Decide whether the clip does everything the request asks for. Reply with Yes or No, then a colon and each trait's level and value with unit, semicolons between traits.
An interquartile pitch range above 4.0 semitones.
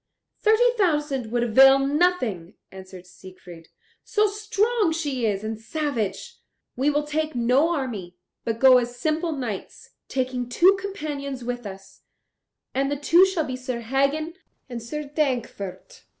Yes: average, 5.2 semitones